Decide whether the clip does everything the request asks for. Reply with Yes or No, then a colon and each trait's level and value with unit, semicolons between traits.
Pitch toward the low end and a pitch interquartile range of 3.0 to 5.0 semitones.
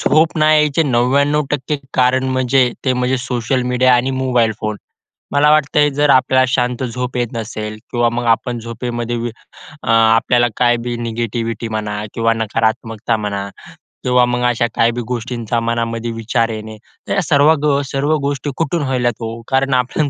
No: low, 125 Hz; narrow, 2.4 semitones